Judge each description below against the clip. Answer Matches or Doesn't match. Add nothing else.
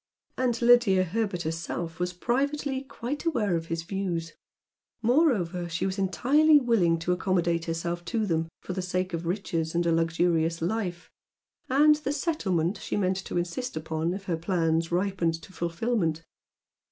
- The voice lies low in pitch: Doesn't match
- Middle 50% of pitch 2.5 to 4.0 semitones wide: Doesn't match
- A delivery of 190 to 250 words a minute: Doesn't match